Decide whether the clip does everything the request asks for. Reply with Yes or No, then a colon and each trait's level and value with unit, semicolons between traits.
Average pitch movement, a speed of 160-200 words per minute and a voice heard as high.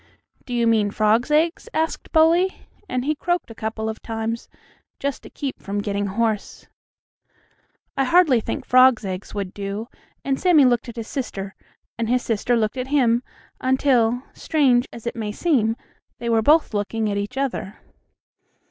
Yes: average, 3.9 semitones; average, 165 wpm; high, 235 Hz